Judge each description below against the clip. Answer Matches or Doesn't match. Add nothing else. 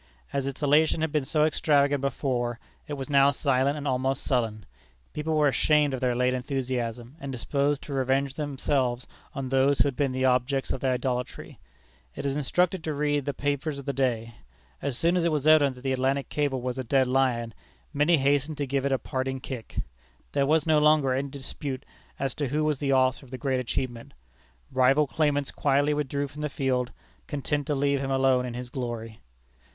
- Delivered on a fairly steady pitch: Matches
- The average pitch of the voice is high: Doesn't match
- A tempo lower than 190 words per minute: Doesn't match